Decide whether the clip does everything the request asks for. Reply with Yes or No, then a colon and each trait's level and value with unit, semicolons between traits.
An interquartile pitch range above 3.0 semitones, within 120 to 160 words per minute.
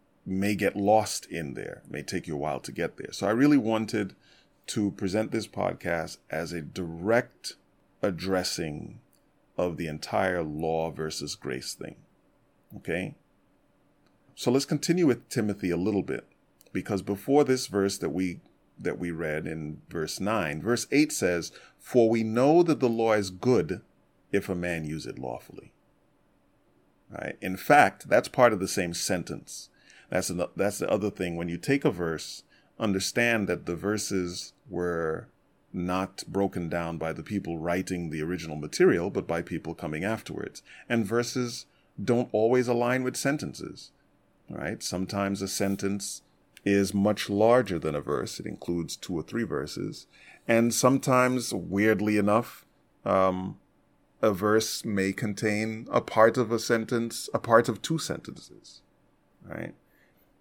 Yes: average, 4.4 semitones; average, 155 wpm